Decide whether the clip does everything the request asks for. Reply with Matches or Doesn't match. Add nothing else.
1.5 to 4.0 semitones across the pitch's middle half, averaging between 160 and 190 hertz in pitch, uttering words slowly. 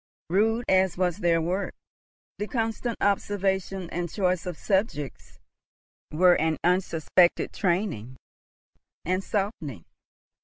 Matches